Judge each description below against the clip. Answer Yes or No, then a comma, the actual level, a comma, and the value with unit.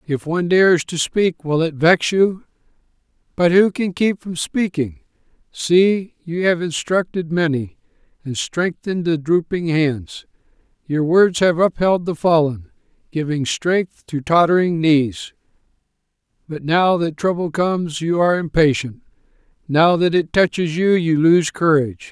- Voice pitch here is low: No, medium, 165 Hz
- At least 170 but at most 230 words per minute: No, average, 140 wpm